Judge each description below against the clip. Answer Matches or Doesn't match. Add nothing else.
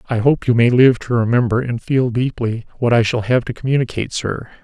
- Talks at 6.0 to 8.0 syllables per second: Doesn't match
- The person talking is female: Doesn't match